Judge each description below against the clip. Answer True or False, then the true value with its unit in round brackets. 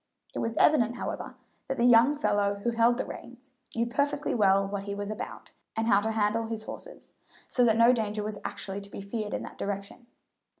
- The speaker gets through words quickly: True (210 wpm)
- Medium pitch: False (225 Hz)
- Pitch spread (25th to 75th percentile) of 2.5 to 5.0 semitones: True (2.9 semitones)